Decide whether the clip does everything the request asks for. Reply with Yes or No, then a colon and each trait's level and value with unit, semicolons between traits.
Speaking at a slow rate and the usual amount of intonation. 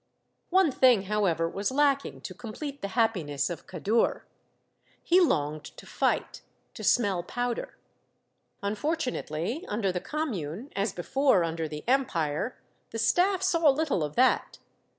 No: slow, 130 wpm; wide, 8.0 semitones